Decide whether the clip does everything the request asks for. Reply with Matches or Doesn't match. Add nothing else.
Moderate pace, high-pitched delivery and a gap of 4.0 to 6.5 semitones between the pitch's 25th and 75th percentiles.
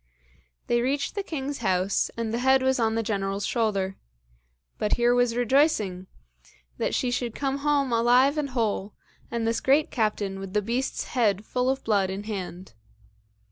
Matches